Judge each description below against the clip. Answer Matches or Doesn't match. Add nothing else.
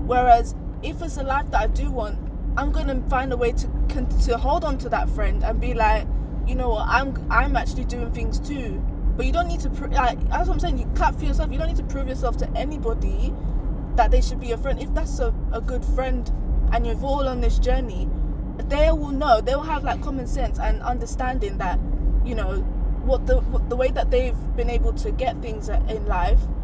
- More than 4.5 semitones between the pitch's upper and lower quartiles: Doesn't match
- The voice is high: Matches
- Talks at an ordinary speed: Doesn't match